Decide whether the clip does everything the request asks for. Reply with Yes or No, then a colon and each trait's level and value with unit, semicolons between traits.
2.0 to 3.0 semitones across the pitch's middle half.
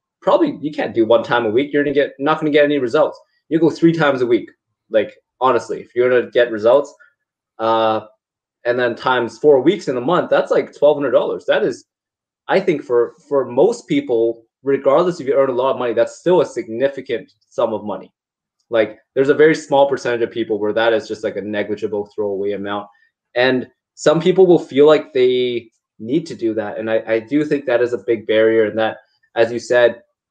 No: wide, 5.6 semitones